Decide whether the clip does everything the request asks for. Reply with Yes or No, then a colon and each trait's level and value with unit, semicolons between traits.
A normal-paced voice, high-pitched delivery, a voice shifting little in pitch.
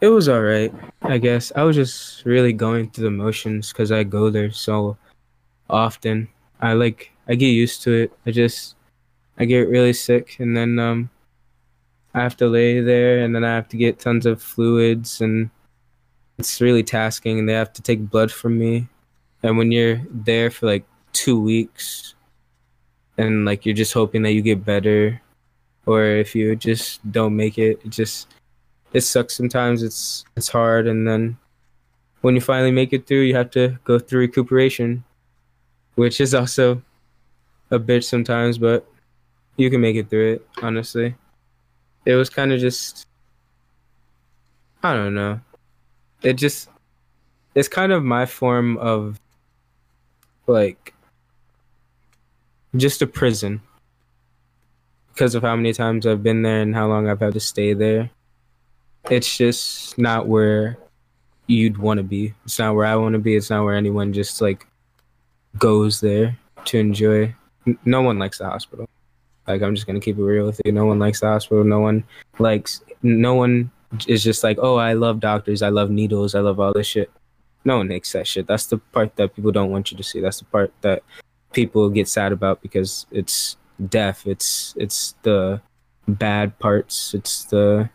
No: average, 175 wpm; low, 115 Hz; narrow, 2.2 semitones